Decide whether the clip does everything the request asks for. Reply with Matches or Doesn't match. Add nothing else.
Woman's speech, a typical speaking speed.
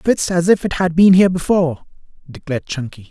Doesn't match